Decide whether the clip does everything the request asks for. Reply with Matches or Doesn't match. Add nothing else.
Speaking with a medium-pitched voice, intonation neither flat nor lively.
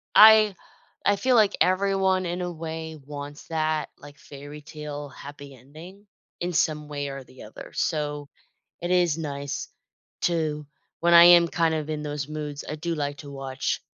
Matches